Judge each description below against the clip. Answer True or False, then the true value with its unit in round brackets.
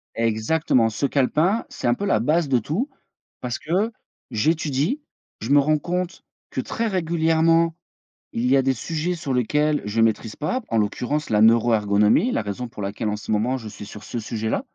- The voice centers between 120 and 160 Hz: True (135 Hz)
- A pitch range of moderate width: False (6.5 semitones)